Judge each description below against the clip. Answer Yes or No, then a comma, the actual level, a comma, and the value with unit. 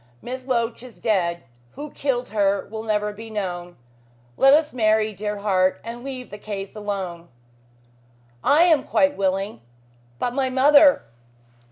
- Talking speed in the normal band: Yes, average, 145 wpm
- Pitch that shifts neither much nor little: Yes, average, 4.7 semitones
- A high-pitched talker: Yes, high, 220 Hz